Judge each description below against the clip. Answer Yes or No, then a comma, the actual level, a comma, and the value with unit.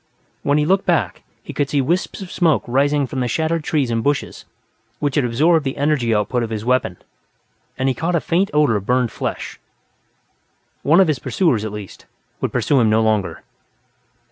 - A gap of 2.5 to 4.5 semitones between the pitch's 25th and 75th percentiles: No, average, 5.2 semitones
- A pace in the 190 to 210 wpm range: Yes, average, 195 wpm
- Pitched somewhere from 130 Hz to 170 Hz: Yes, medium, 140 Hz